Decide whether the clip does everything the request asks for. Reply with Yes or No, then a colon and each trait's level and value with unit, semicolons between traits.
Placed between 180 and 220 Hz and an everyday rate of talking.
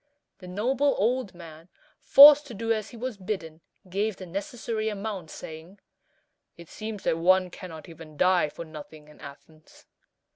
Yes: medium, 185 Hz; average, 155 wpm